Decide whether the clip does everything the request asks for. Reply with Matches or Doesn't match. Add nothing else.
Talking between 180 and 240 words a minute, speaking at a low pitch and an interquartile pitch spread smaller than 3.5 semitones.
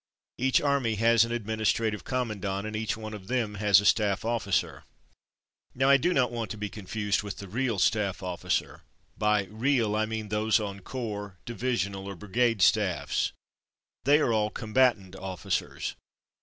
Matches